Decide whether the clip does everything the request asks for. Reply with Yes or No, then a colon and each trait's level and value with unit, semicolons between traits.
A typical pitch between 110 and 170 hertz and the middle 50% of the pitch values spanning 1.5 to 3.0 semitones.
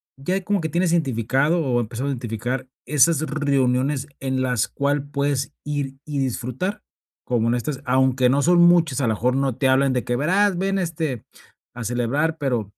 No: low, 135 Hz; average, 3.7 semitones